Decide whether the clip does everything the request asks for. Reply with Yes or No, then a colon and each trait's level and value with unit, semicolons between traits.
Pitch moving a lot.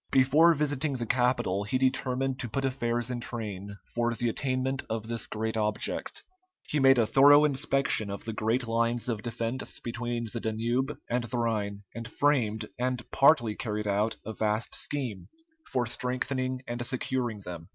No: average, 2.9 semitones